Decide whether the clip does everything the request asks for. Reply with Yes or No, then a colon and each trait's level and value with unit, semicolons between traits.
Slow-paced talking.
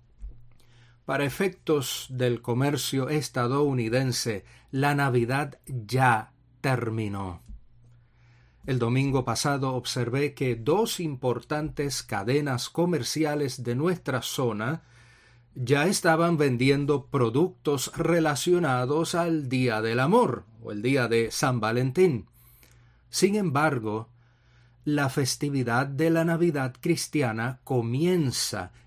Yes: slow, 95 wpm